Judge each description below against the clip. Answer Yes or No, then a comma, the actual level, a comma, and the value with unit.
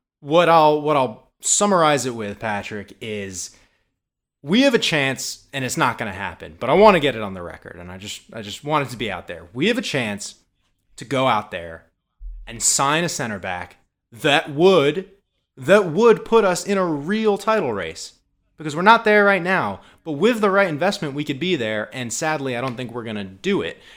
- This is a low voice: No, medium, 150 Hz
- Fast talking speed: Yes, fast, 215 wpm